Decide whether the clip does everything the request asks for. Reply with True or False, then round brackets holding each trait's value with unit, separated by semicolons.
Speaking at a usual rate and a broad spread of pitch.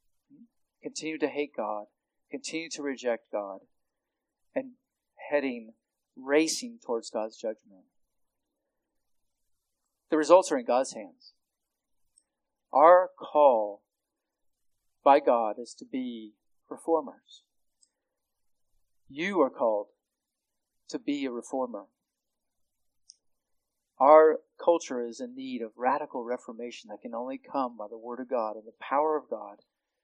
False (115 wpm; 5.8 semitones)